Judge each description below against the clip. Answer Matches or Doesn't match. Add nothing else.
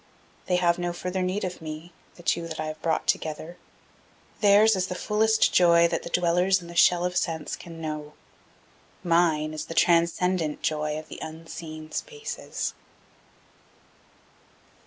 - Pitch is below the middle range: Doesn't match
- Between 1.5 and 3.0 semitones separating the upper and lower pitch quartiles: Matches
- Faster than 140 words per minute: Matches